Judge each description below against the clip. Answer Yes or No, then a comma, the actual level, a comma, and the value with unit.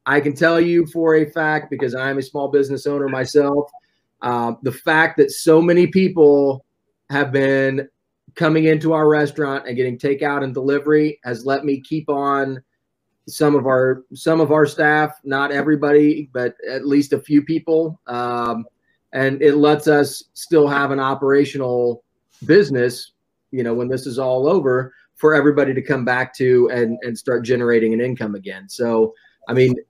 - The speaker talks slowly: No, average, 170 wpm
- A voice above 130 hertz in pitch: Yes, medium, 140 Hz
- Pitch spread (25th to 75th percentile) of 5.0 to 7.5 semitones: No, average, 2.9 semitones